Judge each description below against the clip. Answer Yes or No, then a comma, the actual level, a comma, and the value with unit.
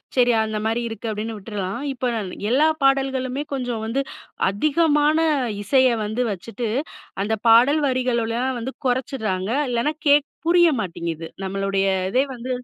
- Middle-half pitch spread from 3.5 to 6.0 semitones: Yes, average, 3.9 semitones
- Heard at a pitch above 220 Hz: Yes, high, 240 Hz